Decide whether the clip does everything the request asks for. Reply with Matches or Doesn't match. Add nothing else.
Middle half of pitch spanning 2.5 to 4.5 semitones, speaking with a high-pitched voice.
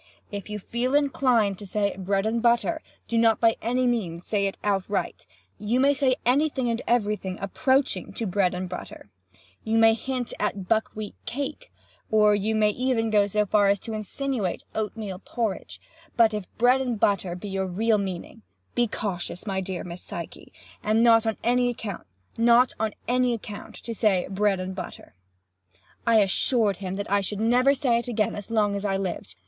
Matches